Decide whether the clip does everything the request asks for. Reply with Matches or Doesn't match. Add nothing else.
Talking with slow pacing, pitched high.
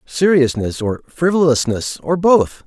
Doesn't match